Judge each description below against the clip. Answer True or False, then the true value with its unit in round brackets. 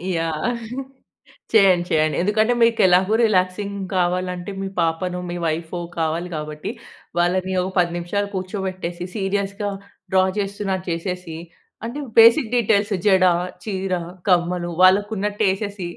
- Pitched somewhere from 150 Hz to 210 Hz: True (185 Hz)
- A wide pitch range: False (2.5 semitones)